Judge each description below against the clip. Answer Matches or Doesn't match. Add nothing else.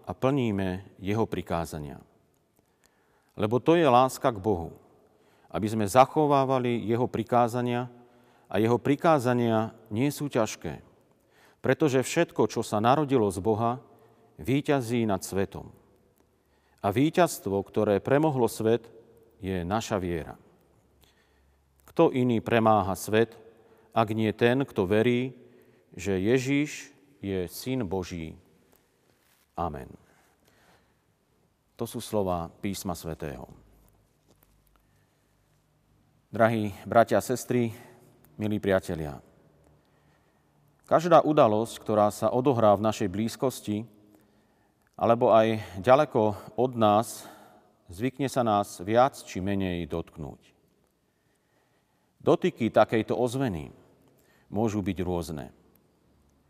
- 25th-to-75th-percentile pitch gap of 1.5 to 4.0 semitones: Doesn't match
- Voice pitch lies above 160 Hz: Doesn't match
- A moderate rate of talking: Doesn't match